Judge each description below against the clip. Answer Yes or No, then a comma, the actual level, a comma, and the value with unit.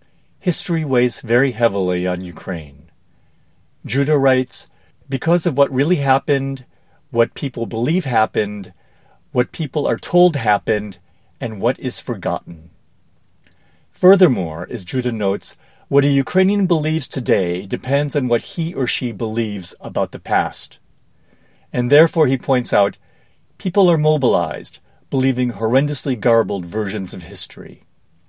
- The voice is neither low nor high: No, low, 130 Hz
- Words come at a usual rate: No, slow, 125 wpm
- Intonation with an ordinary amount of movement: No, wide, 6.1 semitones